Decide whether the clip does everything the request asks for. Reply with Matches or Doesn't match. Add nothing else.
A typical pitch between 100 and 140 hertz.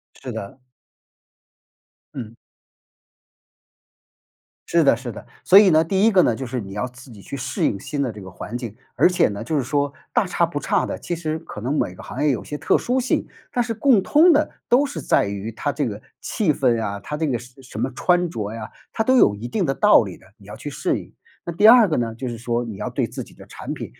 Matches